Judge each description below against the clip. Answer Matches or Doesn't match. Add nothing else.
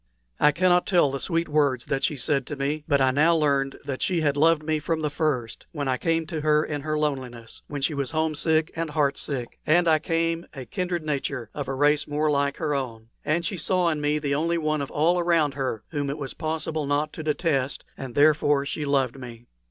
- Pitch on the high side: Doesn't match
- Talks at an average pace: Doesn't match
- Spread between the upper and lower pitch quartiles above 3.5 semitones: Doesn't match